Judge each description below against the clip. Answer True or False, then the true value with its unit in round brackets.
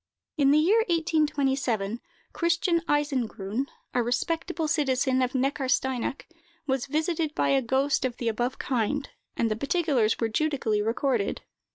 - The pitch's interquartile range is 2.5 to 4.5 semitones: True (4.1 semitones)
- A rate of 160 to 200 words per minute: False (135 wpm)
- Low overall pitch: False (270 Hz)